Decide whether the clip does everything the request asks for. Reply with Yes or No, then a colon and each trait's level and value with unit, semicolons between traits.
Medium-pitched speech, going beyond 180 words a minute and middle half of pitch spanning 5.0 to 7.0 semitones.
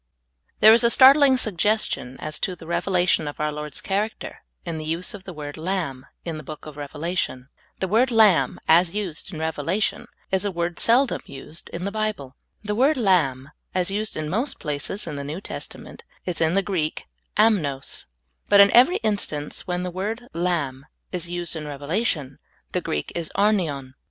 Yes: medium, 175 Hz; average, 190 wpm; average, 5.3 semitones